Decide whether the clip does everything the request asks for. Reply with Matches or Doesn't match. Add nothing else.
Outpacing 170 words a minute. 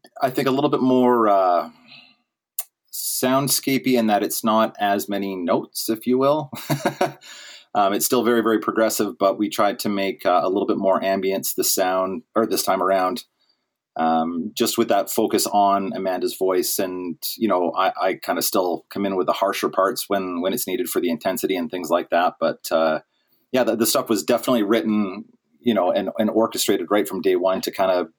Matches